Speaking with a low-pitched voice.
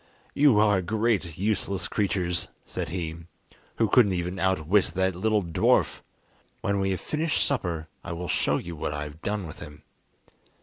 Yes: very low, 95 Hz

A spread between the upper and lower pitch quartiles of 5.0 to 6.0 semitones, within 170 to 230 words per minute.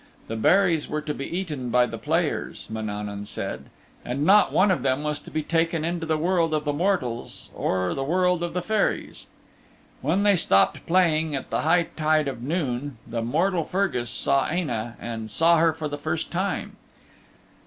Yes: wide, 5.6 semitones; average, 185 wpm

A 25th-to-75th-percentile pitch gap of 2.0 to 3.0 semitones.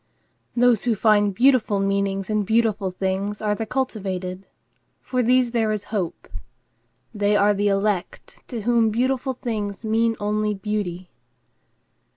Yes: narrow, 2.6 semitones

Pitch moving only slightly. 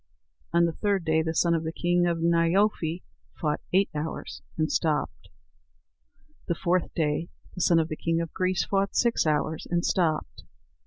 Yes: narrow, 1.9 semitones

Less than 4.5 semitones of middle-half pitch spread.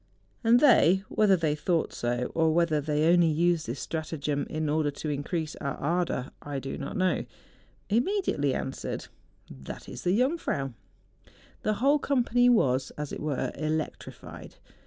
No: average, 4.9 semitones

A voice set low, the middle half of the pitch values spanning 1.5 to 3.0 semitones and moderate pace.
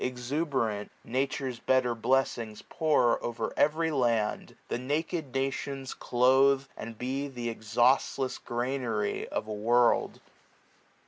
No: low, 125 Hz; narrow, 2.5 semitones; slow, 115 wpm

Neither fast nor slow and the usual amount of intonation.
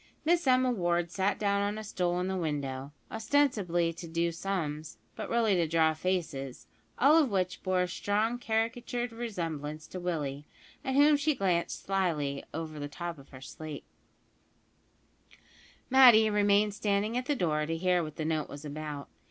No: average, 170 wpm; wide, 5.8 semitones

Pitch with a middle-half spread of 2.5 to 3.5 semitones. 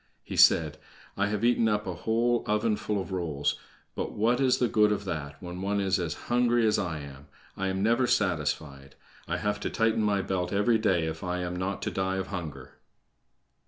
No: average, 4.0 semitones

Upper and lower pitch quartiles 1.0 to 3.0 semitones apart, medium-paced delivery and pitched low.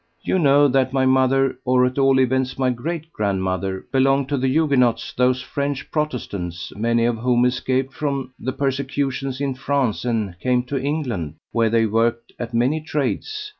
Yes: average, 2.7 semitones; average, 170 wpm; low, 130 Hz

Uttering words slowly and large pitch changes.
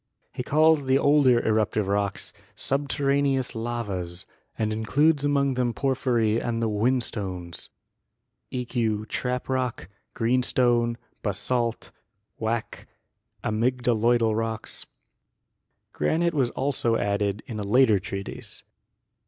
No: slow, 105 wpm; average, 3.4 semitones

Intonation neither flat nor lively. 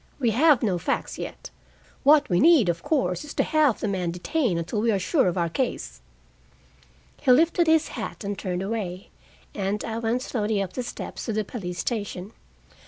No: wide, 6.2 semitones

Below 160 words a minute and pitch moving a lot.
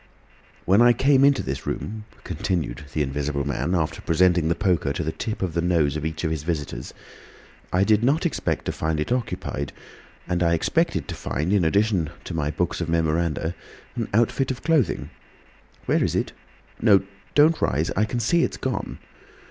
No: average, 180 wpm; wide, 5.9 semitones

